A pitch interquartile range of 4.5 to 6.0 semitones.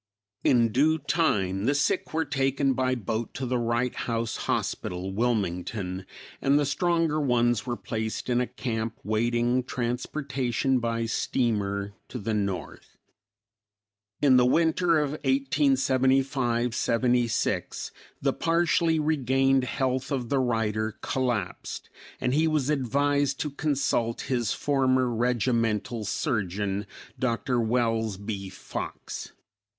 No: average, 3.4 semitones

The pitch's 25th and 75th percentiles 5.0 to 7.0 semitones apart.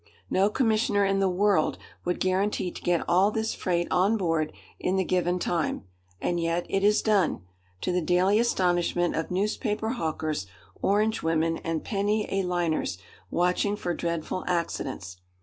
No: average, 3.1 semitones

